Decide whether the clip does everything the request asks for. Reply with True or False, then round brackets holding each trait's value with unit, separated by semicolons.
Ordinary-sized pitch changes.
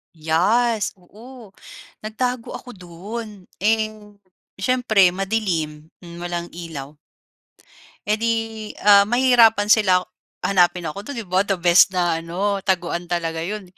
True (4.0 semitones)